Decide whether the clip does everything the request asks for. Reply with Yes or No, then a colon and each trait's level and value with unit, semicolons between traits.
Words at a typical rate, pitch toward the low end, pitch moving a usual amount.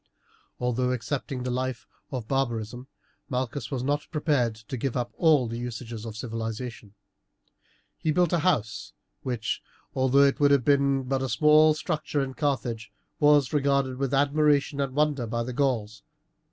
Yes: average, 155 wpm; low, 130 Hz; average, 3.2 semitones